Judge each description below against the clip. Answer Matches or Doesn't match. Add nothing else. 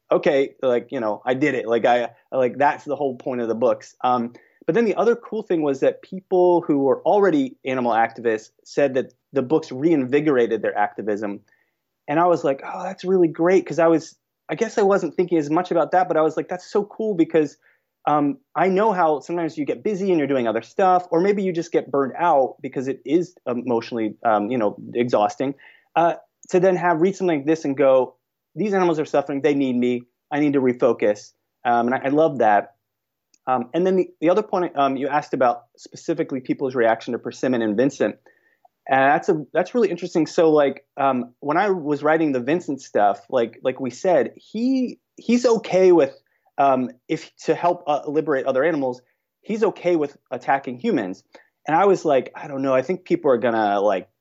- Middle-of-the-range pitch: Matches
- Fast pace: Matches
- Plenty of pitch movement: Matches